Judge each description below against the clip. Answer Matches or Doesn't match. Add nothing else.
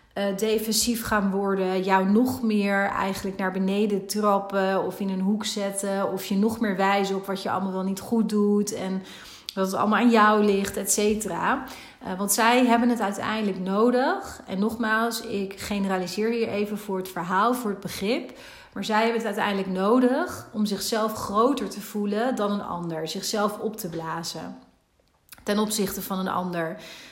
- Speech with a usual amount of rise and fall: Doesn't match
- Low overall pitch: Doesn't match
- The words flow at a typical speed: Matches